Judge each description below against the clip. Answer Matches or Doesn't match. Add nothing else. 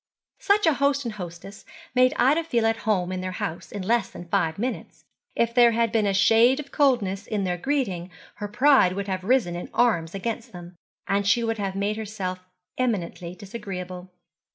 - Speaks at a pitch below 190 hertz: Doesn't match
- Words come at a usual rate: Matches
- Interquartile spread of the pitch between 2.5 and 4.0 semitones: Doesn't match